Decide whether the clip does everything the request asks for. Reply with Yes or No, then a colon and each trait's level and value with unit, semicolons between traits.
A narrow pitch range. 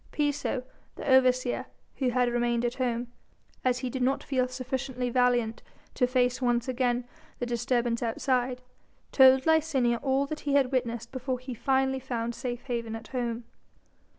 Yes: narrow, 1.6 semitones